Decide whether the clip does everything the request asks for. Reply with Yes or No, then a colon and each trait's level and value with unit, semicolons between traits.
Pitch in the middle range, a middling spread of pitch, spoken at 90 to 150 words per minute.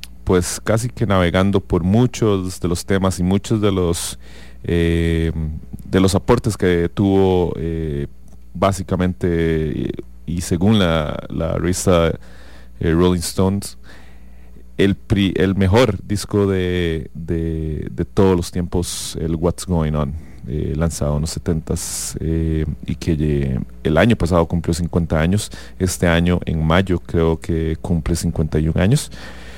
No: very low, 85 Hz; average, 3.1 semitones; average, 140 wpm